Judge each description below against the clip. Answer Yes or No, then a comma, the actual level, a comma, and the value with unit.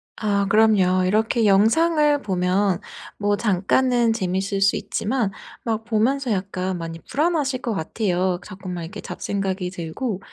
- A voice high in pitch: Yes, high, 205 Hz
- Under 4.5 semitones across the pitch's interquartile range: Yes, average, 3.8 semitones